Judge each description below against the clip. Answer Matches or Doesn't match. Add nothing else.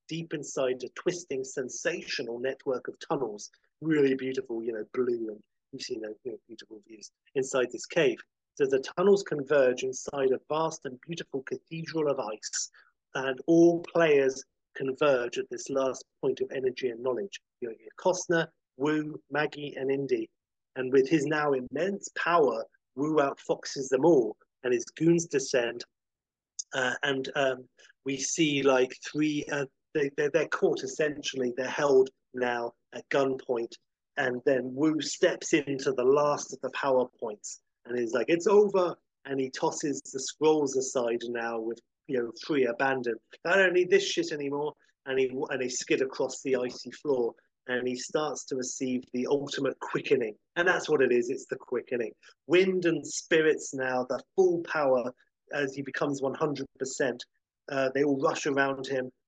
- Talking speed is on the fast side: Doesn't match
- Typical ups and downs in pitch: Doesn't match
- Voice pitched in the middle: Matches